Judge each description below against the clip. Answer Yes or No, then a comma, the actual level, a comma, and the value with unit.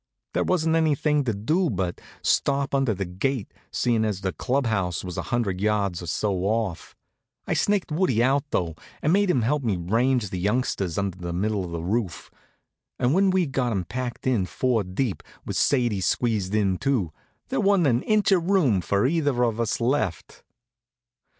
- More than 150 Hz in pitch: No, low, 115 Hz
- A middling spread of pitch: No, wide, 6.4 semitones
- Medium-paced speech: Yes, average, 190 wpm